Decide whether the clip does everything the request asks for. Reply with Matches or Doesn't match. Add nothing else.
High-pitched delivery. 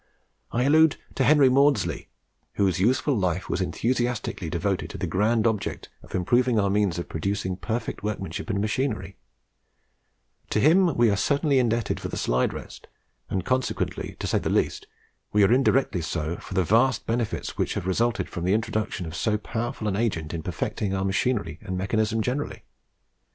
Doesn't match